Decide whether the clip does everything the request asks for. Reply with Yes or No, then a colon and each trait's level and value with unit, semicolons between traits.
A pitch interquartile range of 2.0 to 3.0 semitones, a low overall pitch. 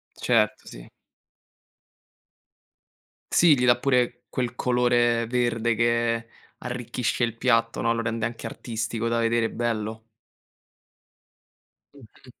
No: narrow, 1.1 semitones; low, 115 Hz